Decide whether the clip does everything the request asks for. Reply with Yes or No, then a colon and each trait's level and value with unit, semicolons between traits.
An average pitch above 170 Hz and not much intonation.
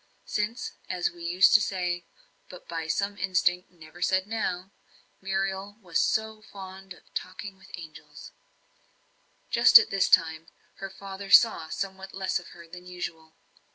Yes: high, 190 Hz; narrow, 1.9 semitones